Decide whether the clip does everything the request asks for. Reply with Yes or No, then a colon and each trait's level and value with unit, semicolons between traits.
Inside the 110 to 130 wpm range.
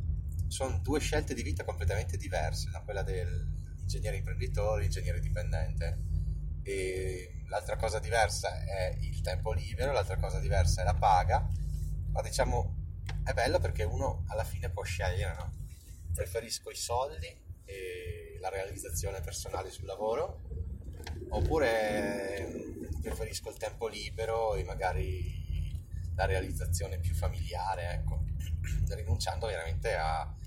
Yes: average, 125 wpm